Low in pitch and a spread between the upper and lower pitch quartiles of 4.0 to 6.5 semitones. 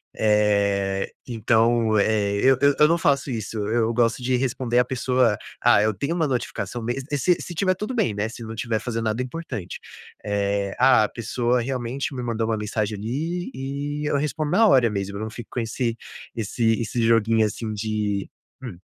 No: low, 115 Hz; average, 3.6 semitones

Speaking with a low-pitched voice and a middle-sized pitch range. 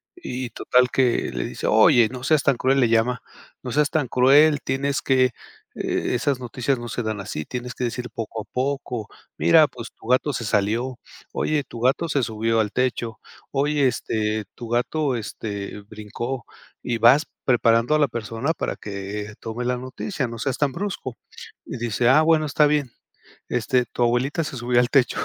Yes: low, 125 Hz; average, 3.1 semitones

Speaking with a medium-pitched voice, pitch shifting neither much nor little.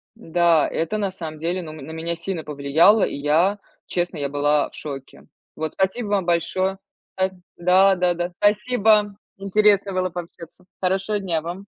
Yes: medium, 180 Hz; average, 3.4 semitones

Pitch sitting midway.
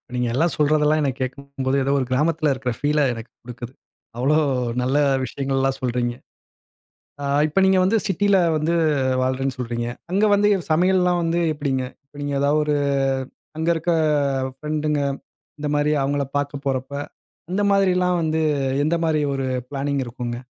Yes: medium, 145 Hz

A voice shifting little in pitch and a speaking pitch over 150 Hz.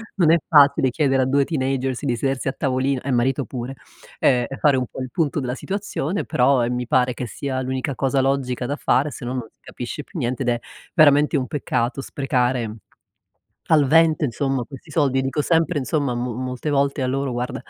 No: narrow, 2.3 semitones; low, 135 Hz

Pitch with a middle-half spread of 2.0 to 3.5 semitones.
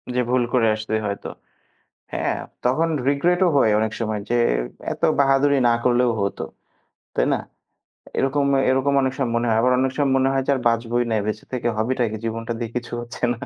Yes: average, 2.8 semitones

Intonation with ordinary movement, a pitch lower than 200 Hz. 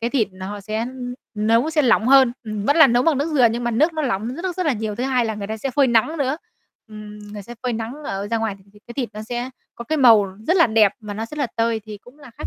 No: average, 4.0 semitones; high, 235 Hz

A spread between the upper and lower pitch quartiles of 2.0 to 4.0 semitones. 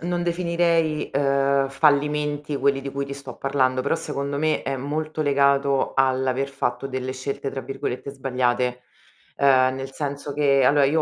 No: narrow, 1.6 semitones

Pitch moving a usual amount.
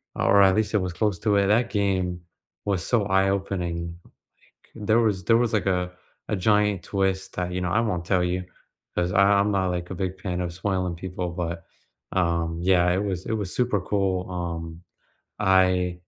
No: narrow, 2.1 semitones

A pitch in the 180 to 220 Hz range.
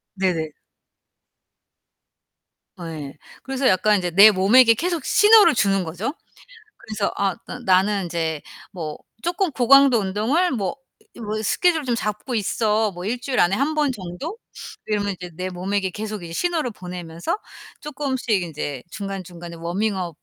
Yes: high, 205 Hz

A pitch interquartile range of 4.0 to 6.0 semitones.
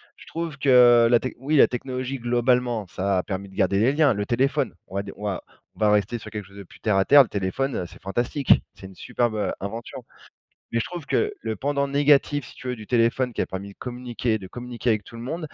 Yes: average, 4.5 semitones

